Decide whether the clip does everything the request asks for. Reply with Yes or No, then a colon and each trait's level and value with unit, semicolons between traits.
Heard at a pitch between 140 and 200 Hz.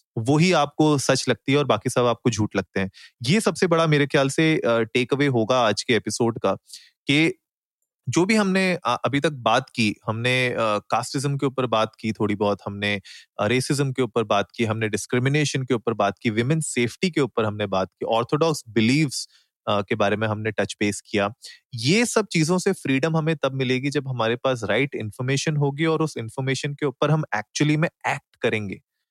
No: low, 130 Hz